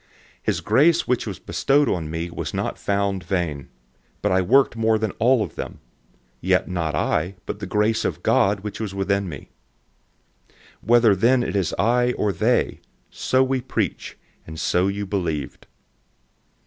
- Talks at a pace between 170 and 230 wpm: No, average, 160 wpm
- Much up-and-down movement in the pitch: No, average, 4.5 semitones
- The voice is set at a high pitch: No, low, 100 Hz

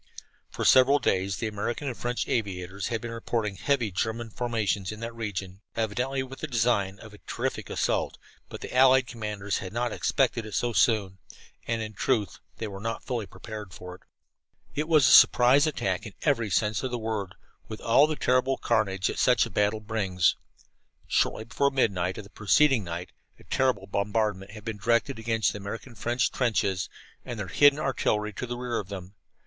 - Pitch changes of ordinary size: Yes, average, 3.5 semitones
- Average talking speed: Yes, average, 190 wpm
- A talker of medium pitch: No, low, 110 Hz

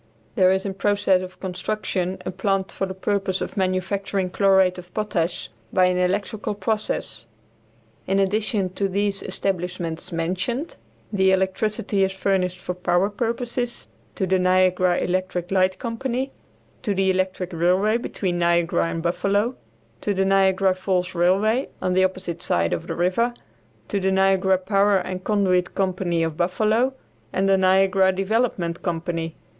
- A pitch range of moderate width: No, narrow, 1.7 semitones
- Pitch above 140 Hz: Yes, high, 190 Hz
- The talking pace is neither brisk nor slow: Yes, average, 150 wpm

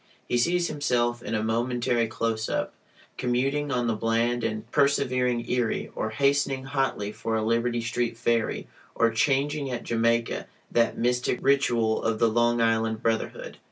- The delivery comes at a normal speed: Yes, average, 155 wpm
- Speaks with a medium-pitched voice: No, low, 120 Hz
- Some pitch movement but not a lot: No, narrow, 2.0 semitones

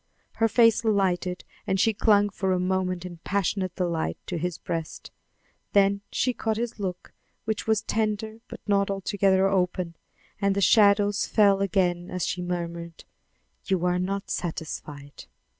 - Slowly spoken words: No, average, 150 wpm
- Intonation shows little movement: Yes, narrow, 2.3 semitones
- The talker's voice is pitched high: Yes, high, 195 Hz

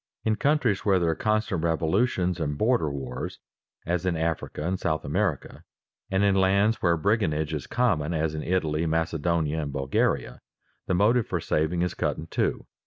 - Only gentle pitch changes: No, average, 4.1 semitones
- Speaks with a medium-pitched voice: No, very low, 85 Hz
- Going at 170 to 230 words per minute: Yes, average, 175 wpm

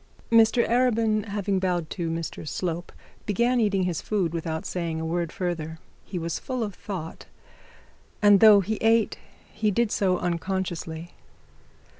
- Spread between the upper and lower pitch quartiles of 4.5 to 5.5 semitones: No, average, 4.1 semitones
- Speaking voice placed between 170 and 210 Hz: Yes, high, 190 Hz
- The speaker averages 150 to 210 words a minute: No, average, 140 wpm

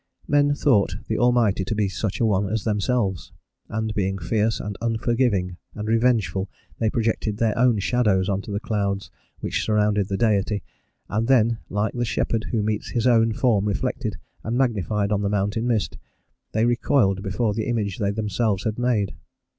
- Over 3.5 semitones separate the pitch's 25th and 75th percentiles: No, narrow, 2.6 semitones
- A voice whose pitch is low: Yes, low, 110 Hz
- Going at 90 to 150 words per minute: No, average, 175 wpm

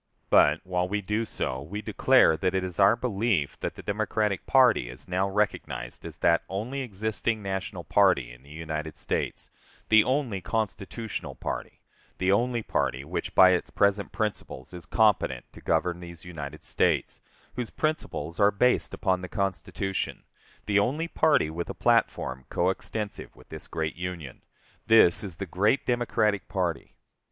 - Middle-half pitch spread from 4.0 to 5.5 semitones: Yes, average, 4.4 semitones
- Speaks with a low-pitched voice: Yes, very low, 95 Hz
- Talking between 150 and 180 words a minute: Yes, average, 160 wpm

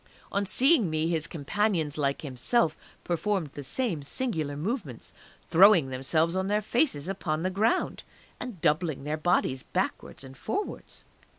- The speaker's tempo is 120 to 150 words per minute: Yes, average, 140 wpm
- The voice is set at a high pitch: No, medium, 165 Hz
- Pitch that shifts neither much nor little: No, wide, 6.0 semitones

